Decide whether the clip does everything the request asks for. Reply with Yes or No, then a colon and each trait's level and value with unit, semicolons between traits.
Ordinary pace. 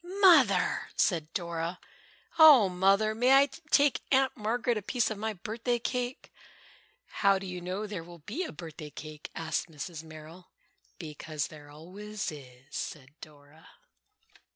Yes: average, 145 wpm